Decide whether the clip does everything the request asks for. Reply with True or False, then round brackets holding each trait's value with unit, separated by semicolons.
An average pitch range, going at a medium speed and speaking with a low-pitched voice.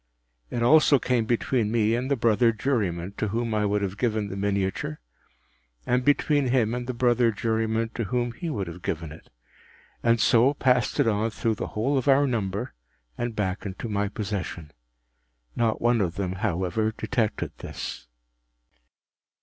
True (3.3 semitones; 170 wpm; 110 Hz)